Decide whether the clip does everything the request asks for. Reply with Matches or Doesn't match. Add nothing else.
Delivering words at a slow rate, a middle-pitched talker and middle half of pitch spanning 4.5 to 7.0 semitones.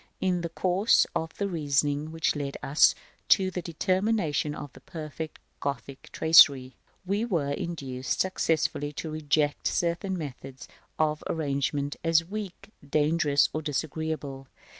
Doesn't match